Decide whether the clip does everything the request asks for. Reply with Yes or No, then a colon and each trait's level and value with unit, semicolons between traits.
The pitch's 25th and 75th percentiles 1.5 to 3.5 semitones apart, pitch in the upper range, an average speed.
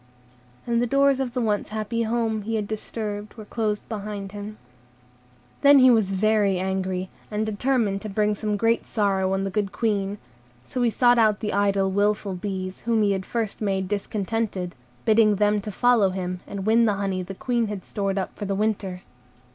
Yes: narrow, 2.4 semitones; high, 210 Hz; average, 185 wpm